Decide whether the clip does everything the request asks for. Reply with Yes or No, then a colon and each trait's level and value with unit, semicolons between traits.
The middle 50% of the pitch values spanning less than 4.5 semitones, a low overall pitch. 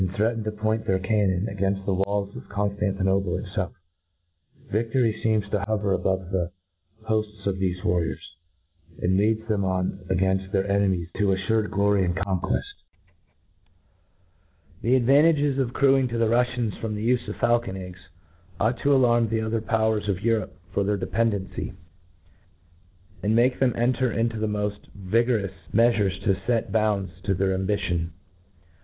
Yes: average, 3.0 semitones; low, 105 Hz